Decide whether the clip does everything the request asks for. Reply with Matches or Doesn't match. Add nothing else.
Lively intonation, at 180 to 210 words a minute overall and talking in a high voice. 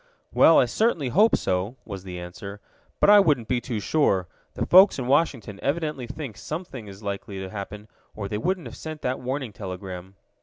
Doesn't match